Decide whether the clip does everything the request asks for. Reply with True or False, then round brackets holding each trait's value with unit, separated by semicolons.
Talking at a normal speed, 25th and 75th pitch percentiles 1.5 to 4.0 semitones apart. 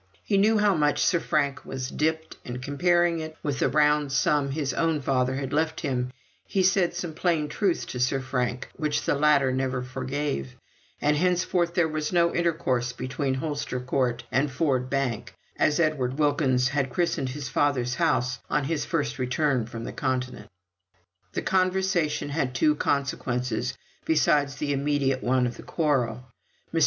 True (170 wpm; 3.6 semitones)